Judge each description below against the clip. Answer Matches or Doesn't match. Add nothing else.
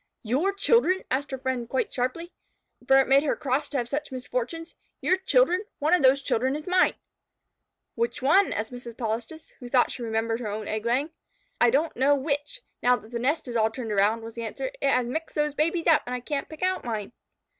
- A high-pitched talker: Matches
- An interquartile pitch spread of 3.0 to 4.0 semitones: Doesn't match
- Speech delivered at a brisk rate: Matches